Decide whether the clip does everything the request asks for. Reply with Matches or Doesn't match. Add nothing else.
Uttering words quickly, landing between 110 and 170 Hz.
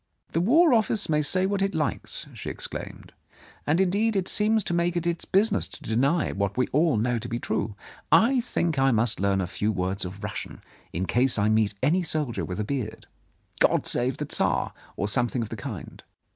Matches